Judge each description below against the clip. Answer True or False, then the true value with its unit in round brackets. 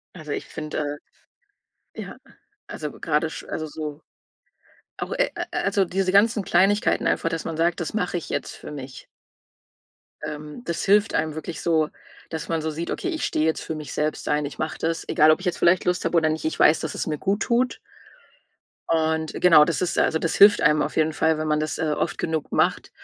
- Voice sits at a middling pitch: True (160 Hz)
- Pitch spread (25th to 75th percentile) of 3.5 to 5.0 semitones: False (2.7 semitones)